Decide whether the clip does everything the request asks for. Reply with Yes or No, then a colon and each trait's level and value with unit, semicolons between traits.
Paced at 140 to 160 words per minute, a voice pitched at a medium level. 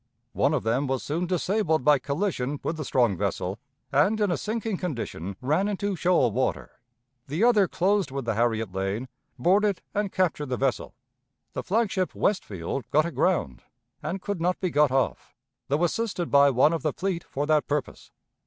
No: average, 180 wpm; medium, 155 Hz